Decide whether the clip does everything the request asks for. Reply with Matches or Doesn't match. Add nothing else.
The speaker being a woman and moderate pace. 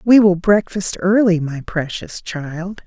Matches